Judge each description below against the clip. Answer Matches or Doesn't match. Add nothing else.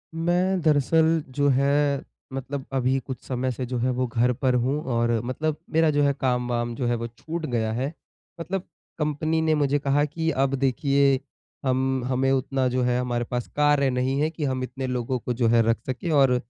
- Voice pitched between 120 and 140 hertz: Matches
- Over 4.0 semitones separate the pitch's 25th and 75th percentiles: Doesn't match